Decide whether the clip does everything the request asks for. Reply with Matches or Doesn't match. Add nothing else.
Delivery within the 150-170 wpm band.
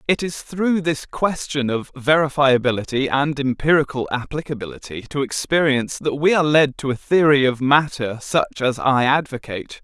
Matches